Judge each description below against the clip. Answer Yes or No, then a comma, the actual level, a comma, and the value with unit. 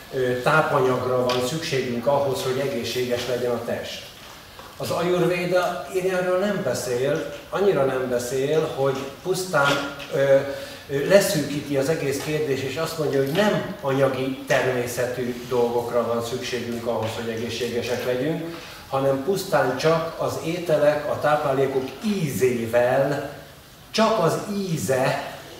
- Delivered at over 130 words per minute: No, average, 115 wpm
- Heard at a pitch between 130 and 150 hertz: Yes, low, 135 Hz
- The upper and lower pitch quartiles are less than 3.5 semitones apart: No, average, 4.5 semitones